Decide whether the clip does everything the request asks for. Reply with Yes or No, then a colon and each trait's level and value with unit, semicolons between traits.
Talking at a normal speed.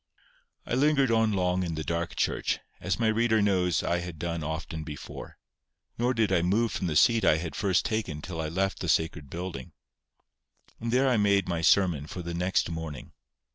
Yes: average, 195 wpm